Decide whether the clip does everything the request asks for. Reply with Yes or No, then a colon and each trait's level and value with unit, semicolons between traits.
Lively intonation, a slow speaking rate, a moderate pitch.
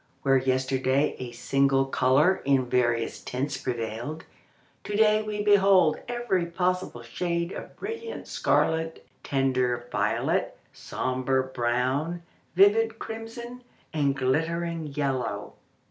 Yes: wide, 6.3 semitones; slow, 105 wpm; medium, 145 Hz